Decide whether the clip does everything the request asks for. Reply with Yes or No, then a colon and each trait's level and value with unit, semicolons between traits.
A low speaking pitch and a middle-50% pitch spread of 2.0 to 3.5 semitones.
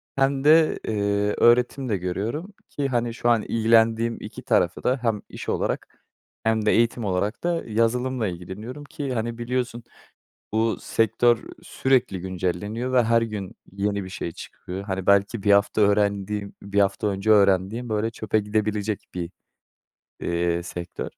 Yes: low, 110 Hz; average, 3.0 semitones